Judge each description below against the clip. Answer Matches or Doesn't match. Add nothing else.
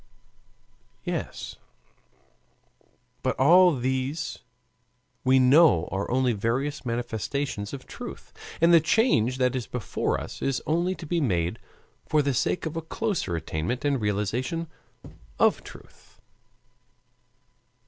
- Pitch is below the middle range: Matches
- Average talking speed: Doesn't match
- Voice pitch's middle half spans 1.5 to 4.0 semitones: Doesn't match